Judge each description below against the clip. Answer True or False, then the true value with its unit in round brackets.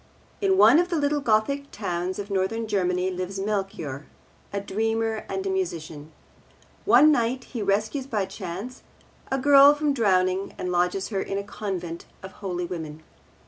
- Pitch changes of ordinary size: False (5.8 semitones)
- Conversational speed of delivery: True (160 wpm)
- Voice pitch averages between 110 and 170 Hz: False (200 Hz)